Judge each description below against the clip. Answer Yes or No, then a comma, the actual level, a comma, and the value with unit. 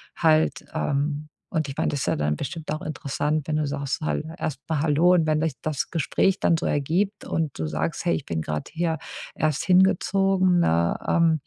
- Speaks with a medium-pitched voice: Yes, medium, 155 Hz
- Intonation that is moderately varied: Yes, average, 3.0 semitones